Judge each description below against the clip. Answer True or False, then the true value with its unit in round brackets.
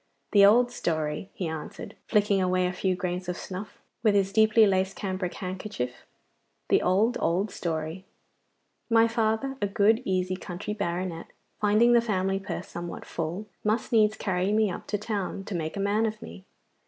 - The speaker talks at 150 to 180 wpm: True (170 wpm)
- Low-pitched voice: False (195 Hz)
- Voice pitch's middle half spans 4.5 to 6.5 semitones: False (2.9 semitones)